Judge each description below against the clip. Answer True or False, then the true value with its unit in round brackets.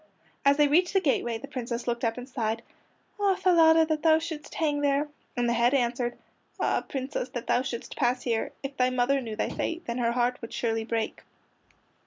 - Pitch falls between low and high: False (255 Hz)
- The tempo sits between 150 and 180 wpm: False (205 wpm)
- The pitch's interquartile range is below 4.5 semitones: True (3.8 semitones)